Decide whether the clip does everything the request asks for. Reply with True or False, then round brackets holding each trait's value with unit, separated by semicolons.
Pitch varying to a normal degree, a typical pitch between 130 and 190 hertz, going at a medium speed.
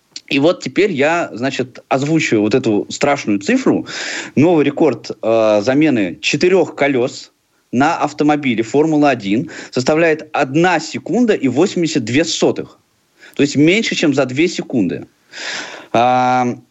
True (3.7 semitones; 140 Hz; 120 wpm)